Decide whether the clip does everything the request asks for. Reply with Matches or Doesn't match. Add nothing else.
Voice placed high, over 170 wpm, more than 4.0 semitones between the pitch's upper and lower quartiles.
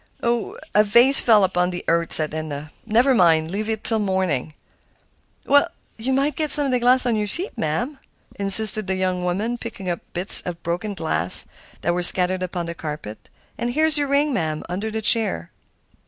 Matches